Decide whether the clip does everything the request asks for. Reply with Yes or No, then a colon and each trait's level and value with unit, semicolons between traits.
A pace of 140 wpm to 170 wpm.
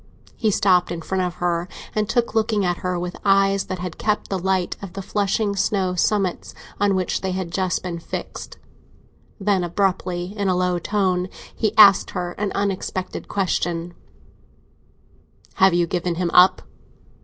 Yes: average, 165 wpm